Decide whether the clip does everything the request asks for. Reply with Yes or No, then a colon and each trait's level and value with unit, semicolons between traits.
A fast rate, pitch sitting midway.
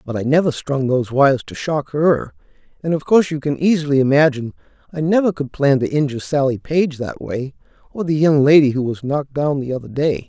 Yes: fast, 215 wpm; medium, 145 Hz